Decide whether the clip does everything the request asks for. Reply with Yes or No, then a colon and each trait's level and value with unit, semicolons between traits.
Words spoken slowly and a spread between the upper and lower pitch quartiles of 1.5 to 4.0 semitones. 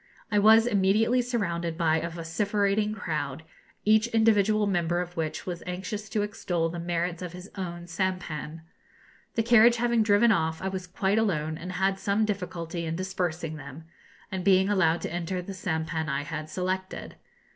No: average, 170 wpm; average, 3.7 semitones